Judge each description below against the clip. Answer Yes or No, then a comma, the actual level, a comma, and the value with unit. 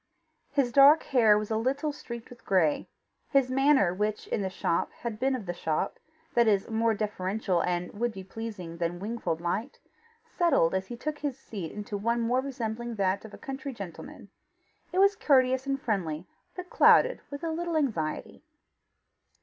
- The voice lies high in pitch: Yes, high, 230 Hz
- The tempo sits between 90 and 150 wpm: No, average, 175 wpm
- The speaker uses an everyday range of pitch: No, wide, 5.9 semitones